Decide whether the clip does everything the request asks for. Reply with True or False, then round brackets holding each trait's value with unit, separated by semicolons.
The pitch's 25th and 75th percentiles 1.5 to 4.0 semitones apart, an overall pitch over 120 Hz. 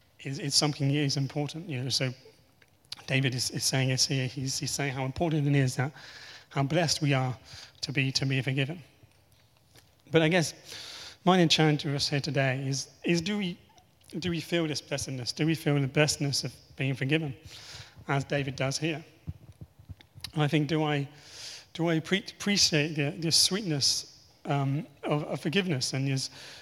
True (2.8 semitones; 140 Hz)